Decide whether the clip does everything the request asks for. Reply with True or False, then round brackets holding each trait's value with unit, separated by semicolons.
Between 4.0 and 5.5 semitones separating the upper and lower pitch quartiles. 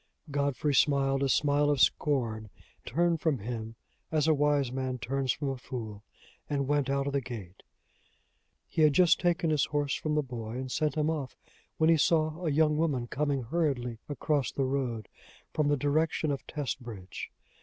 False (3.2 semitones)